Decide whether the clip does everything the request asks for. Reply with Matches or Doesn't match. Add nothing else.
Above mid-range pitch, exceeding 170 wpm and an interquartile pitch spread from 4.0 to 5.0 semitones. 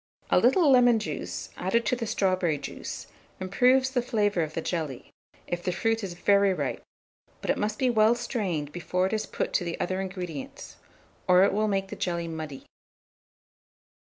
Matches